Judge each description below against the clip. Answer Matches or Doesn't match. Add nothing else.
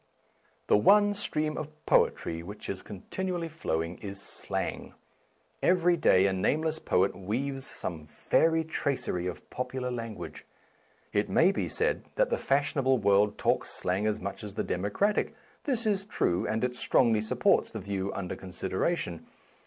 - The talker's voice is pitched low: Matches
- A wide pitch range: Matches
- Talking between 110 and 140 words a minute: Doesn't match